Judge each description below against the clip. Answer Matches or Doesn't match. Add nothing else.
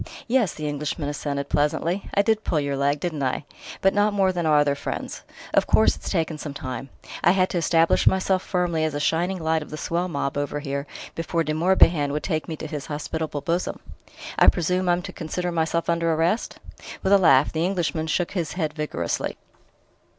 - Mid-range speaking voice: Matches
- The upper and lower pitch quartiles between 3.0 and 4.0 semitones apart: Matches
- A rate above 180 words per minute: Matches